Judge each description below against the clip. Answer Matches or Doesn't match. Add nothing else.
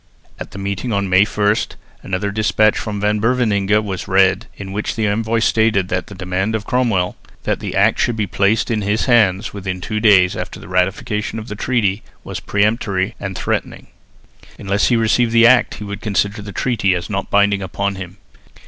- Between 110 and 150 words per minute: Doesn't match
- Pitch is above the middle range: Doesn't match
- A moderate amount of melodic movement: Doesn't match